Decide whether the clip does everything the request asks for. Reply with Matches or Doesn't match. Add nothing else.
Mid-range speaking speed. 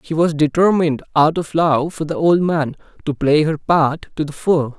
Doesn't match